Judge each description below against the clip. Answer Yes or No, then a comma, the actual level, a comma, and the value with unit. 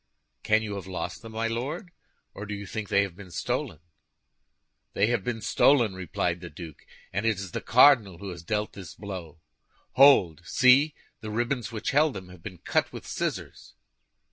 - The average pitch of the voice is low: Yes, low, 100 Hz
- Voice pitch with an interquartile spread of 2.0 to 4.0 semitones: No, average, 4.4 semitones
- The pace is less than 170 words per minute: No, average, 185 wpm